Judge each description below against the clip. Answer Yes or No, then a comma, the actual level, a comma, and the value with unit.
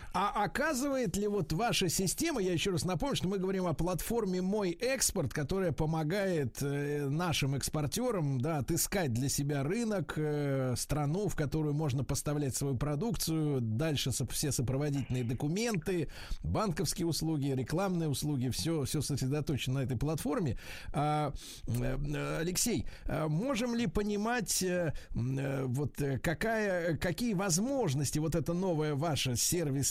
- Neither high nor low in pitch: Yes, medium, 155 Hz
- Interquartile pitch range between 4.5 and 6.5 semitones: Yes, average, 4.8 semitones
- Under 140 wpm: Yes, average, 120 wpm